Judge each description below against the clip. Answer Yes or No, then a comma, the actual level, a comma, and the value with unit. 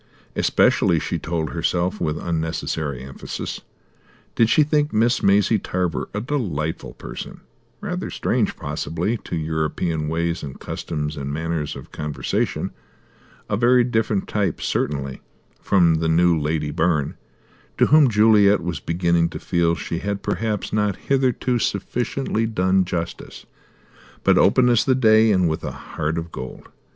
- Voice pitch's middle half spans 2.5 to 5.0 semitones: No, wide, 5.4 semitones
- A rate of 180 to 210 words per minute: No, average, 140 wpm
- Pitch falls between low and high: No, very low, 90 Hz